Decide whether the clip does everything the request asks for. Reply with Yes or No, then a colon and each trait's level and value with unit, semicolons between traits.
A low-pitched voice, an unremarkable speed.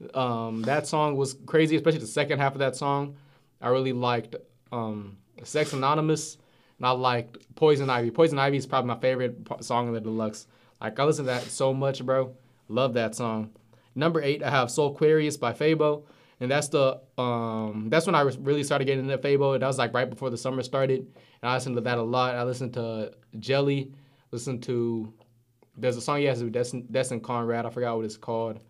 No: low, 130 Hz; fast, 210 wpm